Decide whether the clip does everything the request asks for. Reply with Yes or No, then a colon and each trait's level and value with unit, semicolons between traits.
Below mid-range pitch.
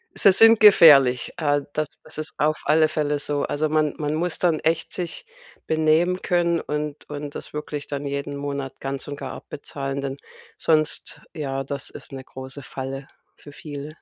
No: medium, 150 Hz